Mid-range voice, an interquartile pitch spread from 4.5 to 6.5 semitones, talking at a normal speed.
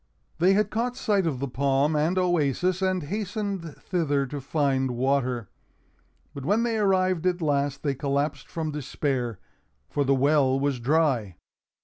Yes: medium, 150 Hz; average, 5.2 semitones; average, 150 wpm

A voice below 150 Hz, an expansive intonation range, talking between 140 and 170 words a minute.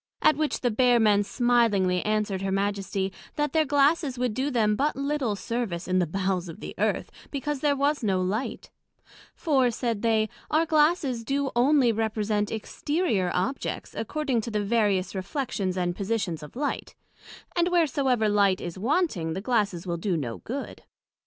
No: high, 225 Hz; wide, 6.1 semitones; average, 165 wpm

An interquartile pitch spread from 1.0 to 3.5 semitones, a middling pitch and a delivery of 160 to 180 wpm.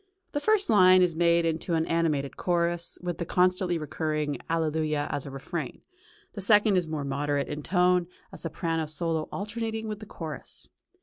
Yes: average, 3.0 semitones; medium, 170 Hz; average, 170 wpm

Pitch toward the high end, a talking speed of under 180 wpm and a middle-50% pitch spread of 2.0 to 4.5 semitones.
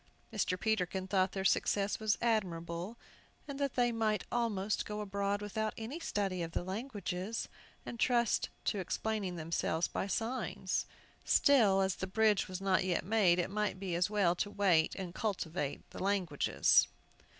Yes: high, 200 Hz; average, 160 wpm; average, 3.0 semitones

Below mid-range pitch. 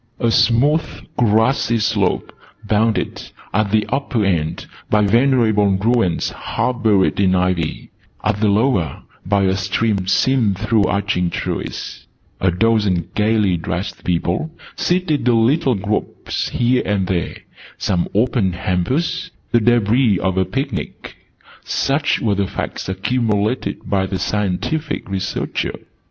Yes: low, 105 Hz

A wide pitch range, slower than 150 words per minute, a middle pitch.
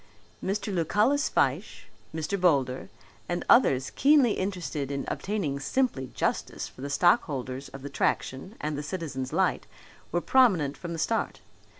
Yes: wide, 6.6 semitones; average, 140 wpm; medium, 165 Hz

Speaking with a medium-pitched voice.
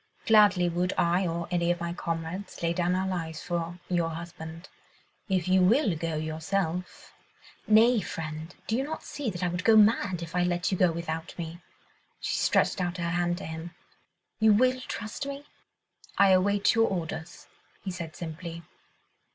Yes: medium, 175 Hz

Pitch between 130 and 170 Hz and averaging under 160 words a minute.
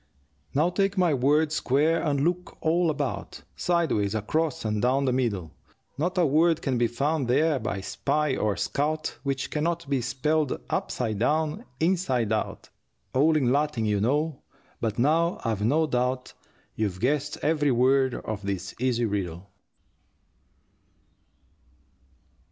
Yes: medium, 140 Hz; average, 140 wpm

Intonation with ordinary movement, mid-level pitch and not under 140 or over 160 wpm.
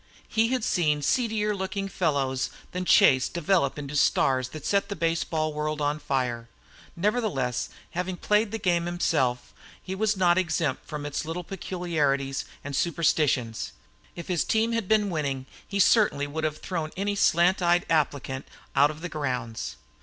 Yes: average, 4.9 semitones; medium, 165 Hz; average, 155 wpm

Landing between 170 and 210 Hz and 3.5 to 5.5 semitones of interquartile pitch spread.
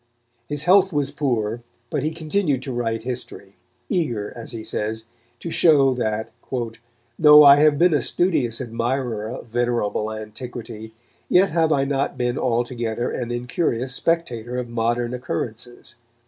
No: low, 125 Hz; average, 4.1 semitones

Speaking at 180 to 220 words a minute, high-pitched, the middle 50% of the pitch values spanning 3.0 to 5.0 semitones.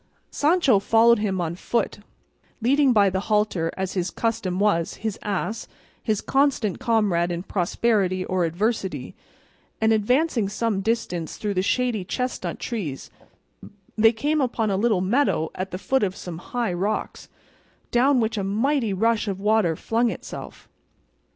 No: average, 150 wpm; high, 215 Hz; average, 3.9 semitones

